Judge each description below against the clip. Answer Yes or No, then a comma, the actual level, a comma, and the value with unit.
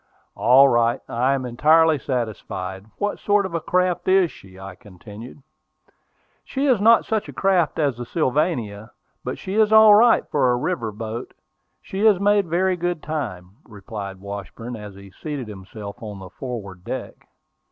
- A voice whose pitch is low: Yes, low, 125 Hz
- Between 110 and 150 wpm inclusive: No, average, 165 wpm